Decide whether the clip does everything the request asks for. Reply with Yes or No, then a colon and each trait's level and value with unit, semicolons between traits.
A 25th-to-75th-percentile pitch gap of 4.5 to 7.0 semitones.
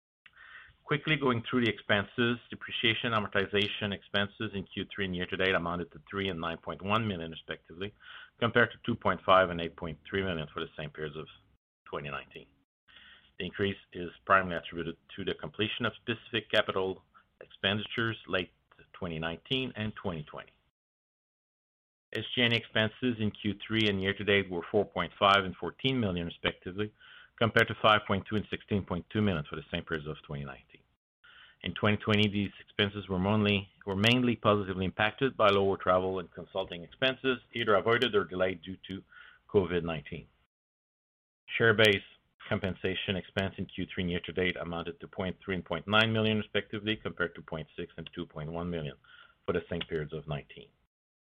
No: average, 3.8 semitones